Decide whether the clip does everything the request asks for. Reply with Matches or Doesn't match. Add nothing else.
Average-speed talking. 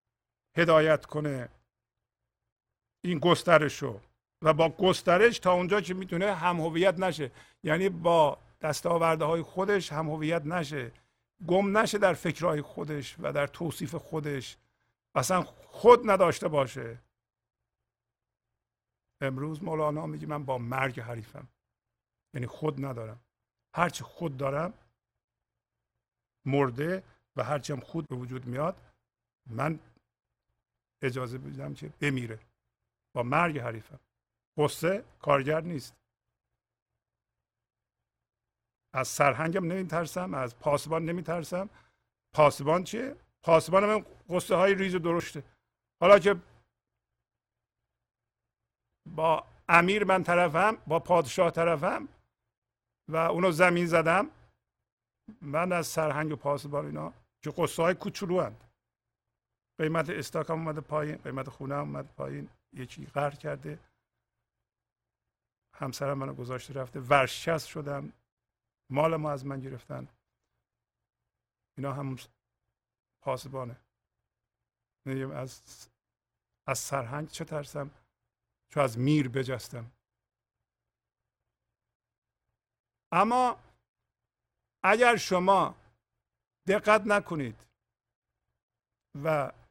Doesn't match